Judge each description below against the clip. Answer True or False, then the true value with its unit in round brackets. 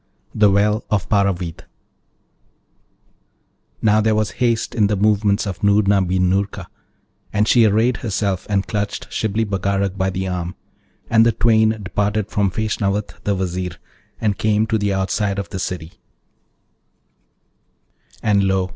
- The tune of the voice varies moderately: False (2.0 semitones)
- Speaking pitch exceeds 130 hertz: False (100 Hz)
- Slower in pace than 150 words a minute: True (140 wpm)